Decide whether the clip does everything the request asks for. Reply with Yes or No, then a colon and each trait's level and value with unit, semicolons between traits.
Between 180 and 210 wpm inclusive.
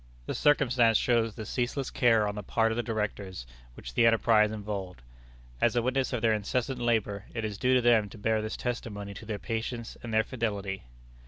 Yes: average, 200 wpm